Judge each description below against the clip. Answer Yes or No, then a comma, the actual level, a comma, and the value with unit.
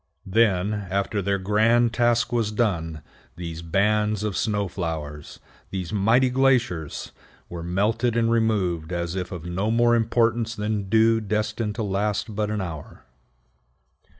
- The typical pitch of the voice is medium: No, low, 105 Hz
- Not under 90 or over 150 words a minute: Yes, average, 140 wpm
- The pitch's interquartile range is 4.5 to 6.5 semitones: No, average, 3.9 semitones